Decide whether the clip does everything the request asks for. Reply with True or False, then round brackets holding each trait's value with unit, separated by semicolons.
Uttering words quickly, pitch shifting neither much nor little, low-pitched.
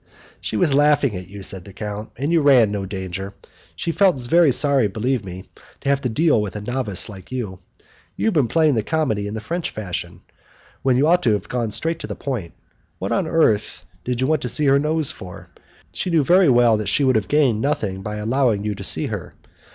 False (230 wpm; 6.1 semitones; 125 Hz)